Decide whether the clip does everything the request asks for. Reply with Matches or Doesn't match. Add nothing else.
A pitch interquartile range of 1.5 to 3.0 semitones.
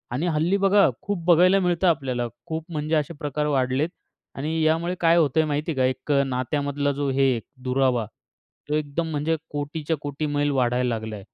Doesn't match